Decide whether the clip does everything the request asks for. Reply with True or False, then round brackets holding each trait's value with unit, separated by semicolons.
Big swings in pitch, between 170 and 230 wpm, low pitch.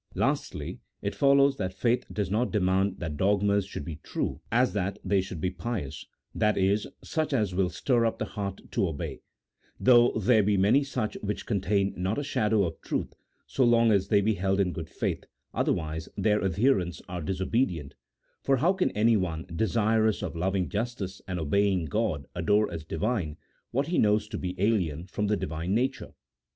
False (3.7 semitones; 185 wpm; 100 Hz)